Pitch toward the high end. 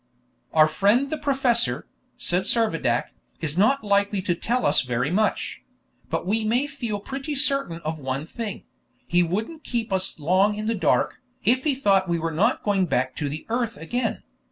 Yes: high, 205 Hz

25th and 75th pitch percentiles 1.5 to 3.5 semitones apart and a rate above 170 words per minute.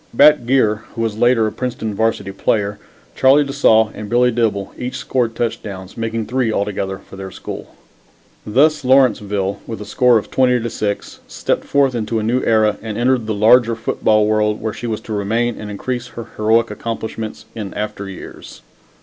Yes: narrow, 2.6 semitones; average, 180 wpm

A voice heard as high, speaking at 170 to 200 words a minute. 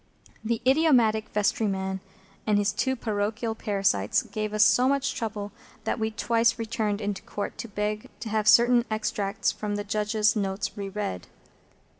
No: high, 215 Hz; average, 155 wpm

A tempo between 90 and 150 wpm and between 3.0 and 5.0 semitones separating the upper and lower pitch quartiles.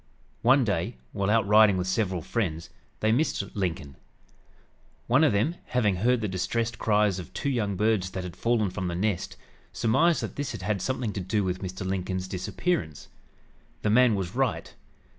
No: average, 175 wpm; average, 4.0 semitones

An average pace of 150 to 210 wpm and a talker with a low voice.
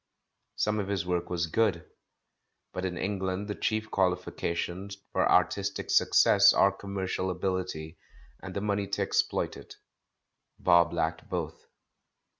No: slow, 135 wpm; very low, 95 Hz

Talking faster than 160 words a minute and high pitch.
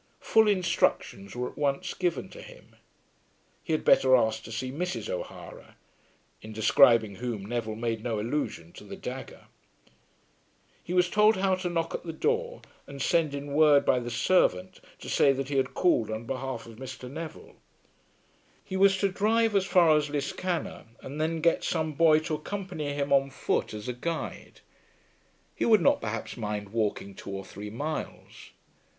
No: average, 175 wpm; medium, 140 Hz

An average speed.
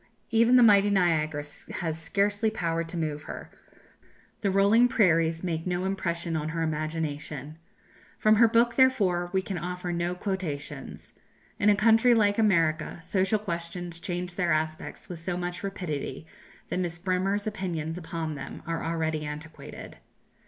Yes: average, 150 wpm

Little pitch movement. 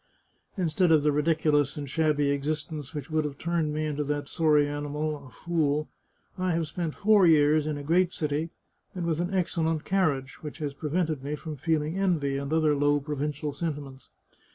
Yes: narrow, 2.0 semitones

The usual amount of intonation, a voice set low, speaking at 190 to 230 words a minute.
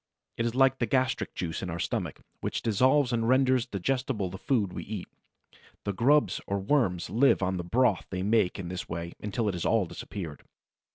No: wide, 5.7 semitones; low, 105 Hz; average, 195 wpm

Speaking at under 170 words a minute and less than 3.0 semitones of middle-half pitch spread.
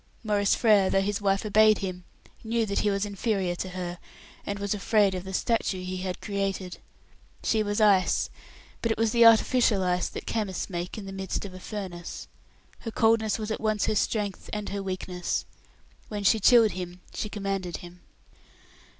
No: average, 185 wpm; narrow, 2.5 semitones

